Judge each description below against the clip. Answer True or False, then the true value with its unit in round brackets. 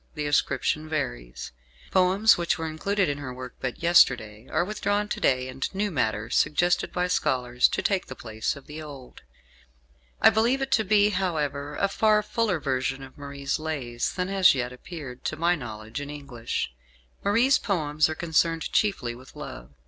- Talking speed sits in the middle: True (175 wpm)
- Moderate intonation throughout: False (6.4 semitones)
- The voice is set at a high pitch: False (150 Hz)